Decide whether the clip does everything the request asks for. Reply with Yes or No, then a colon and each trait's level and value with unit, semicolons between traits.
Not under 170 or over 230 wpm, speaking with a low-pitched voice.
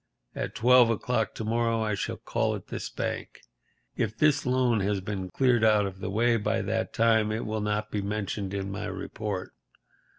Yes: average, 190 wpm; low, 110 Hz